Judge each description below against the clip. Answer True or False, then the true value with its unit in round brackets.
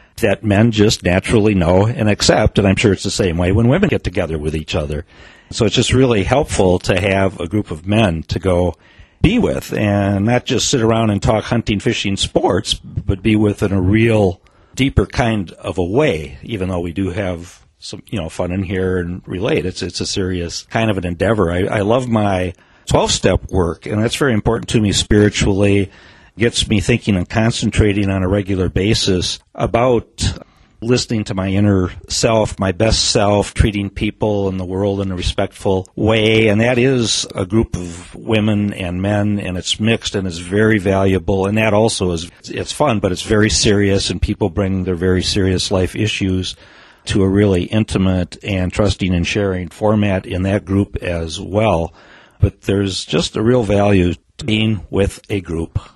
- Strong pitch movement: False (2.8 semitones)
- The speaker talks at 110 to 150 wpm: False (190 wpm)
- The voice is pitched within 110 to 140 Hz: False (100 Hz)